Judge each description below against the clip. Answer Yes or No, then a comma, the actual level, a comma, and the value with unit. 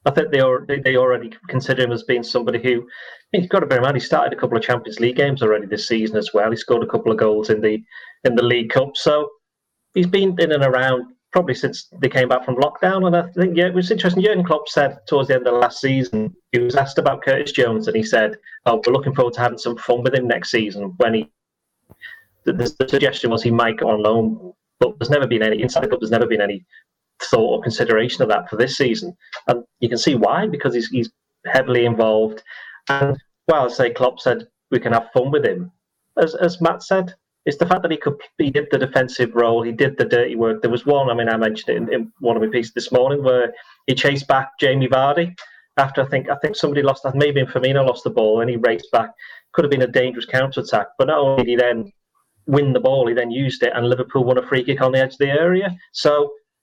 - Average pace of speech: No, fast, 250 wpm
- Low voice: Yes, low, 130 Hz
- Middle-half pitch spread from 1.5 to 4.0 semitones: Yes, average, 3.3 semitones